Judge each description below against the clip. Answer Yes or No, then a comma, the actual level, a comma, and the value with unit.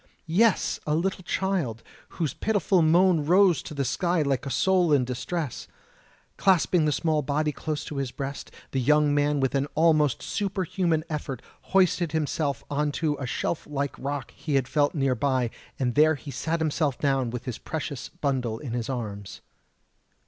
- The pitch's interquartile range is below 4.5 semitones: Yes, average, 3.5 semitones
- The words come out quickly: No, average, 170 wpm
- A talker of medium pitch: Yes, medium, 150 Hz